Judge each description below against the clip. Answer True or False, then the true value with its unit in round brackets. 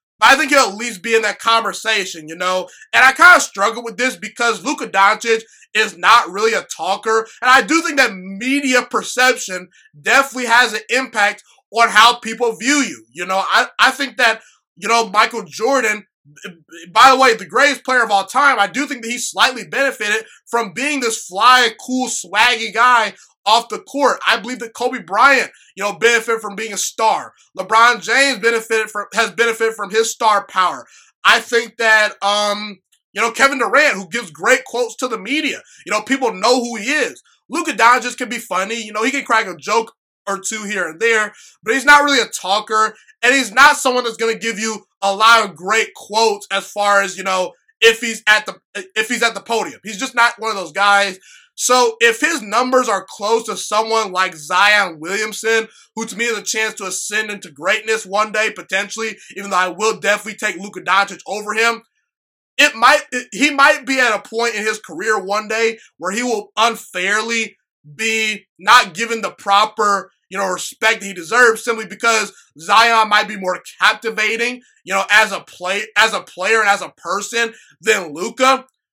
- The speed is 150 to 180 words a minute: False (200 wpm)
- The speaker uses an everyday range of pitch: True (3.2 semitones)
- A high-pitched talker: True (225 Hz)